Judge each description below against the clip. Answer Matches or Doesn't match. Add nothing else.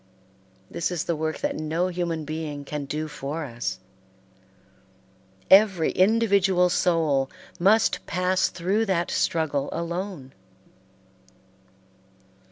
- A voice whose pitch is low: Doesn't match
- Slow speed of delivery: Matches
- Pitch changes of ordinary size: Matches